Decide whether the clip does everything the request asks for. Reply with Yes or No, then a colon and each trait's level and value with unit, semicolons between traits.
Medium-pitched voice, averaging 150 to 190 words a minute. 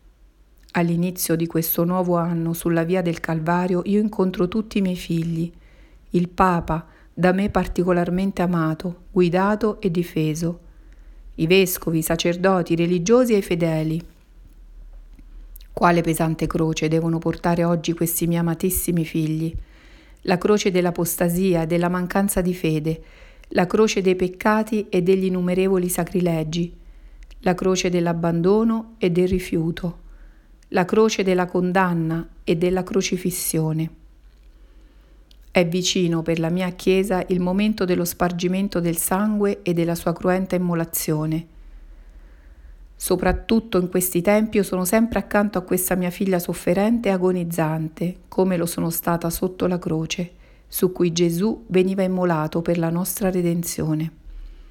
No: medium, 175 Hz; average, 130 wpm